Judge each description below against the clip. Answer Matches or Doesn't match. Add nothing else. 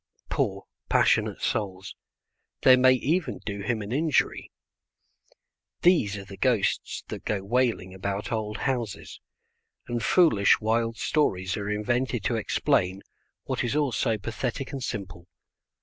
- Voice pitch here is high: Doesn't match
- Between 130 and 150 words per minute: Matches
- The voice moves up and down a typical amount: Matches